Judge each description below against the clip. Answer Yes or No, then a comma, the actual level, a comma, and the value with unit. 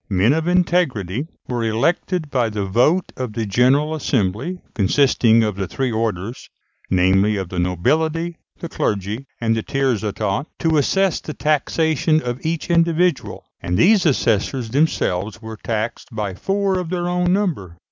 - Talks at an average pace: Yes, average, 155 wpm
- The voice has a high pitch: No, low, 125 Hz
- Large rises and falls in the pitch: Yes, wide, 7.5 semitones